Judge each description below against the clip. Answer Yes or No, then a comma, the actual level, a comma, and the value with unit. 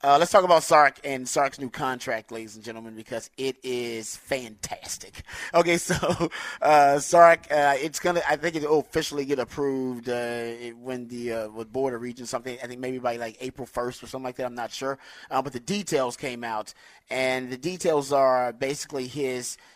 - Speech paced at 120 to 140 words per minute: No, average, 190 wpm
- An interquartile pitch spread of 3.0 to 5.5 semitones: Yes, average, 3.3 semitones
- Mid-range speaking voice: No, low, 130 Hz